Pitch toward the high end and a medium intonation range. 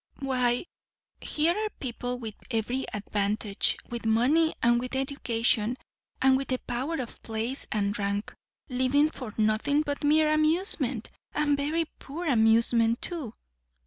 Yes: very high, 255 Hz; average, 4.4 semitones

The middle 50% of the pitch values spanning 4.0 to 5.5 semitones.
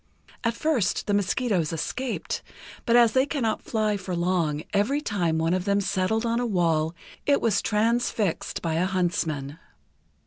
Yes: average, 5.1 semitones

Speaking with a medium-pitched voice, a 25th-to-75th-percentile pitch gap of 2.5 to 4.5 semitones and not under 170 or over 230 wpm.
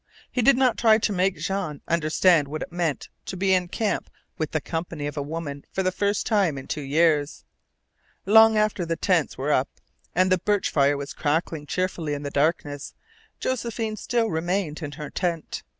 No: medium, 170 Hz; average, 4.9 semitones; average, 190 wpm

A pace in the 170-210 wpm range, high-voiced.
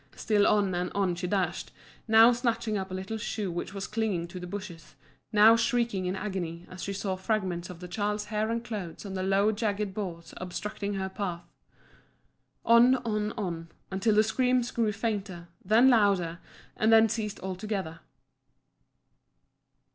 No: average, 160 wpm; high, 200 Hz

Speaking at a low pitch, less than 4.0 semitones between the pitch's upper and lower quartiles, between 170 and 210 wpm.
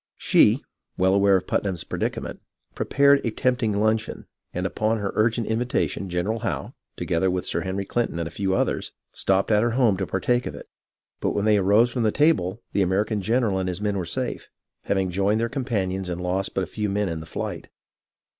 Yes: low, 100 Hz; average, 3.2 semitones; fast, 205 wpm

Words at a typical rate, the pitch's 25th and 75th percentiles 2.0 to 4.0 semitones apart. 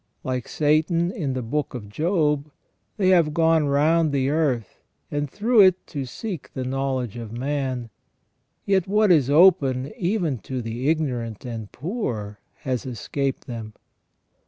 No: average, 145 wpm; average, 4.8 semitones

